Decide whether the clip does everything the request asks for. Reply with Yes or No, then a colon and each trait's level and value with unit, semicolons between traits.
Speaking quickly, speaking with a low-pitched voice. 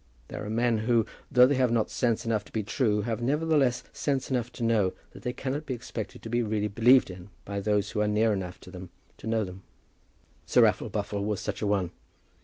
Yes: fast, 220 wpm; low, 110 Hz